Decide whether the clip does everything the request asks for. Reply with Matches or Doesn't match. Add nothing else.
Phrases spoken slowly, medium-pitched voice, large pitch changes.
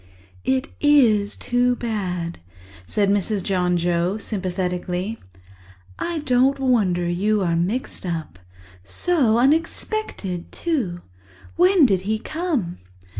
Doesn't match